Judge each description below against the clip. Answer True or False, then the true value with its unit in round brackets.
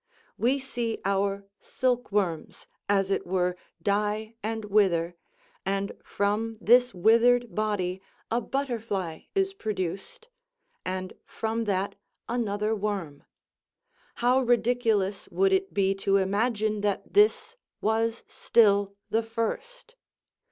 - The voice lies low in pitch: False (215 Hz)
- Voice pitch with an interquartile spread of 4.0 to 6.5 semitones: False (3.4 semitones)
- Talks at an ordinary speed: False (110 wpm)